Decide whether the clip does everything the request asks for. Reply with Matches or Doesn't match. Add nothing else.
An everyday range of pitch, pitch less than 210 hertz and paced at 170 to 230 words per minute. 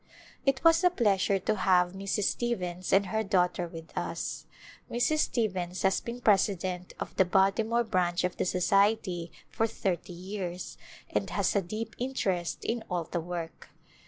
Doesn't match